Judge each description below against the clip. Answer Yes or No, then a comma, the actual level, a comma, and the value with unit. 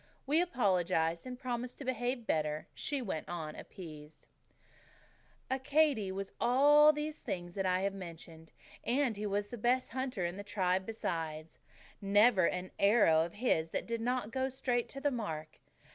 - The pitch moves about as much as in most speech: No, wide, 6.5 semitones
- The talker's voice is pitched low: No, high, 205 Hz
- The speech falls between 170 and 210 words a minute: No, average, 160 wpm